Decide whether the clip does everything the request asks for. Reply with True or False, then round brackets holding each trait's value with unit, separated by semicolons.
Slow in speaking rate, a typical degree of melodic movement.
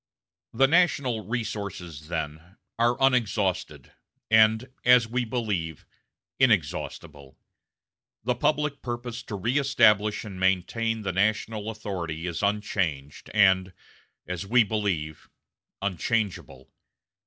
True (95 wpm; 4.9 semitones)